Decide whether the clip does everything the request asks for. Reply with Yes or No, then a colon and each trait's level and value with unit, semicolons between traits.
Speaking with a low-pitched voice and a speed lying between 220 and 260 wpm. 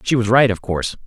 No: low, 110 Hz; fast, 280 wpm